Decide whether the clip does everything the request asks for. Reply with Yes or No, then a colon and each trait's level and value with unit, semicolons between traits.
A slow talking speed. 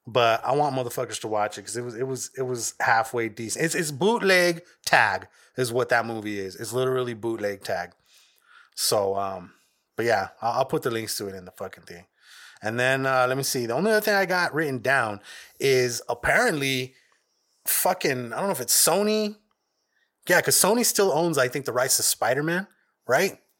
No: fast, 205 wpm